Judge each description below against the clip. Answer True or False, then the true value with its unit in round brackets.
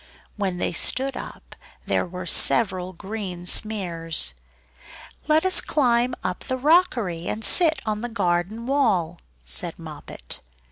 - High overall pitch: True (205 Hz)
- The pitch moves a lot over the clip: True (6.0 semitones)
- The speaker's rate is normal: False (130 wpm)